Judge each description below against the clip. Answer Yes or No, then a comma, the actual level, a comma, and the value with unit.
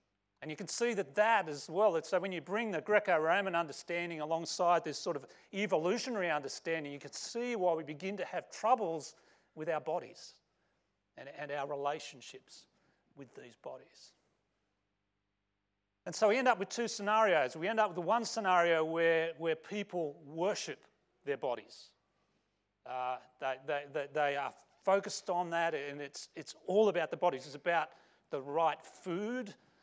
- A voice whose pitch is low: No, medium, 165 Hz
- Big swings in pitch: Yes, wide, 5.9 semitones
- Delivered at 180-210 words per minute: No, average, 165 wpm